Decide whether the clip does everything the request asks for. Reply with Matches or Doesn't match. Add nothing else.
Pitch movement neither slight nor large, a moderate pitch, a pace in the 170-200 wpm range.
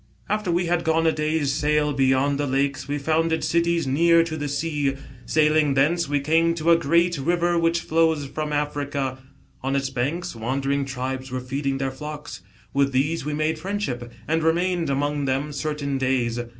Matches